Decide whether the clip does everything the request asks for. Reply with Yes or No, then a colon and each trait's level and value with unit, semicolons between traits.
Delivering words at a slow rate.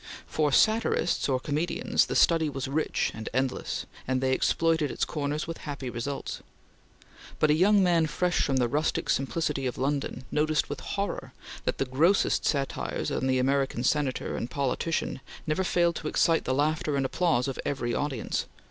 No: average, 170 wpm